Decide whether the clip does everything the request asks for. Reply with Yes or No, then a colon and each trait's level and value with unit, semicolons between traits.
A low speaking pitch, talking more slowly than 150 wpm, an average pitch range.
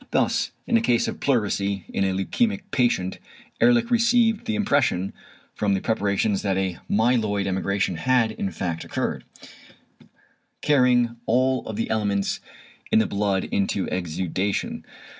Yes: low, 105 Hz; average, 140 wpm; average, 4.7 semitones